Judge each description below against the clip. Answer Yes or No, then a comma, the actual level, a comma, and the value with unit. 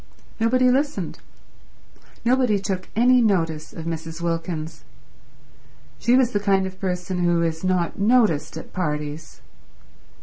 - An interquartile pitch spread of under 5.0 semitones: No, wide, 5.6 semitones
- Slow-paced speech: Yes, slow, 125 wpm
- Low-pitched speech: No, medium, 185 Hz